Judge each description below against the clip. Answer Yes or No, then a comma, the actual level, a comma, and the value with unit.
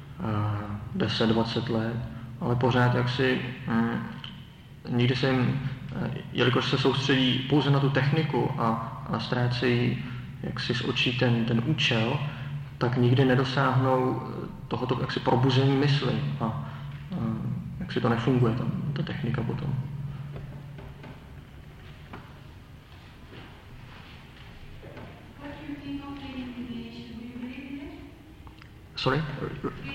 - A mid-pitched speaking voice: No, low, 130 Hz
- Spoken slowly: Yes, slow, 90 wpm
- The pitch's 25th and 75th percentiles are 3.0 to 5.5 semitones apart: No, narrow, 2.5 semitones